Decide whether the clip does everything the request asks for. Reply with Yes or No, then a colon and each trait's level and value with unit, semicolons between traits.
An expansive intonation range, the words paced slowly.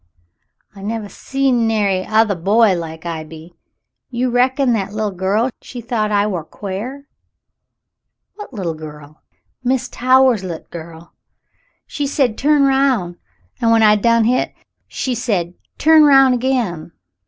No: wide, 6.0 semitones; average, 165 wpm